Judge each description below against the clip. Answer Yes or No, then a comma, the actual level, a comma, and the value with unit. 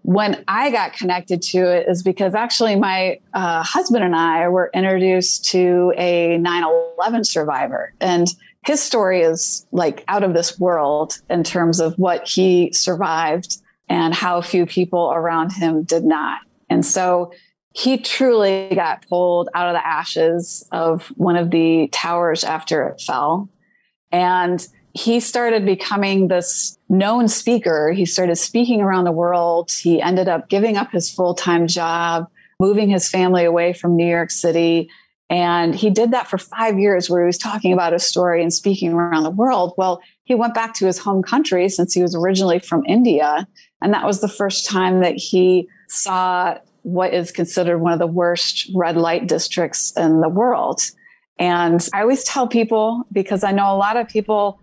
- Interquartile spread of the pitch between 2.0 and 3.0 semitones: Yes, average, 2.7 semitones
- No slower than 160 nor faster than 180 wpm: Yes, average, 175 wpm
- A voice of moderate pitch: Yes, medium, 180 Hz